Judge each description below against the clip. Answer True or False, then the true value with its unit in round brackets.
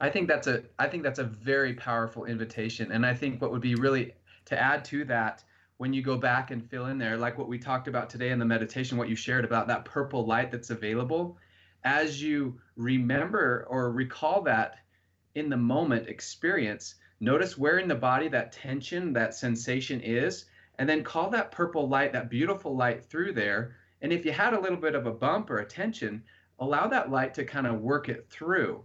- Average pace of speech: False (210 wpm)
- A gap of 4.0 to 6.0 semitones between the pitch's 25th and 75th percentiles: False (3.4 semitones)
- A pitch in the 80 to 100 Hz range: False (125 Hz)